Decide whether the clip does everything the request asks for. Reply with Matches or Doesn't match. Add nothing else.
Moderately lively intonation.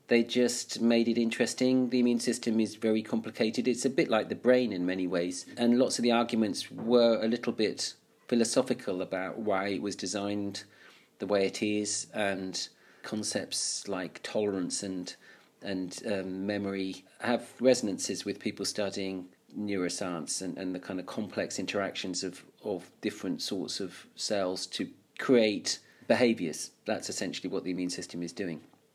Matches